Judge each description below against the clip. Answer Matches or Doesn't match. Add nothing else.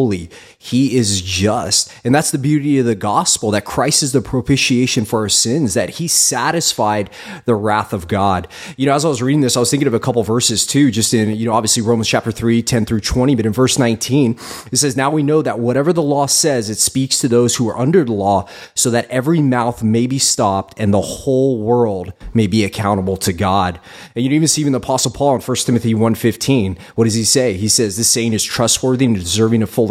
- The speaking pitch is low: Matches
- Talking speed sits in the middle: Doesn't match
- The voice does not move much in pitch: Doesn't match